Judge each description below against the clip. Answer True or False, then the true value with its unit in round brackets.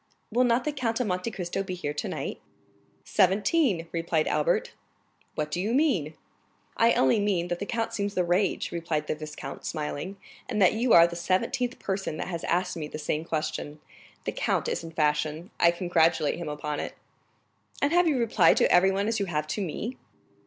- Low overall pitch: False (180 Hz)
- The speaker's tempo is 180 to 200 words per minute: True (190 wpm)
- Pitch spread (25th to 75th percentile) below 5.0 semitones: False (5.5 semitones)